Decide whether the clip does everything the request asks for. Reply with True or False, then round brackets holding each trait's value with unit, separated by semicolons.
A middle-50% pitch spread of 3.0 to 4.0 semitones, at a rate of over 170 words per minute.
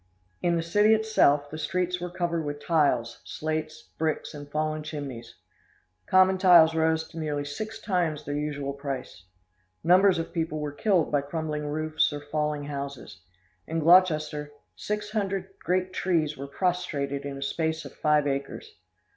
False (3.5 semitones; 155 wpm)